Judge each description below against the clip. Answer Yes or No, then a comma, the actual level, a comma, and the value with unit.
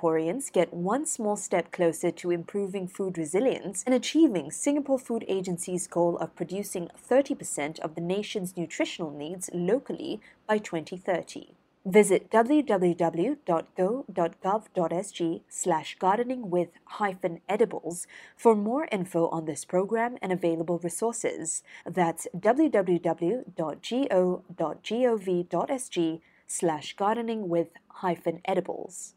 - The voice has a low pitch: No, medium, 185 Hz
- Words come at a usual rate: No, slow, 100 wpm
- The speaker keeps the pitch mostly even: No, average, 3.9 semitones